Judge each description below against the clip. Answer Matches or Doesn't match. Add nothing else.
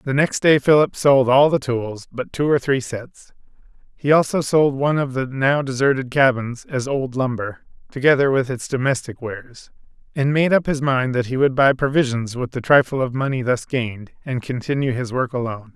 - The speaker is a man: Matches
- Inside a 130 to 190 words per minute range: Doesn't match